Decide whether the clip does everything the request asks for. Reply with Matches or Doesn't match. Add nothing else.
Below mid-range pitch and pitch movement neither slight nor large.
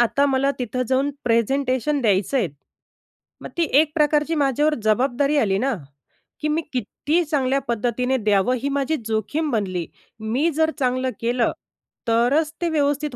Doesn't match